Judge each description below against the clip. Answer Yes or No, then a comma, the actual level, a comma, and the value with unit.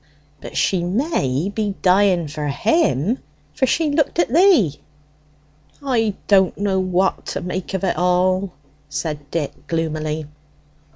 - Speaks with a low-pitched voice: No, medium, 185 Hz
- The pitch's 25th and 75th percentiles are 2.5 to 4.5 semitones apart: No, average, 5.1 semitones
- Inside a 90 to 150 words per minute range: Yes, slow, 135 wpm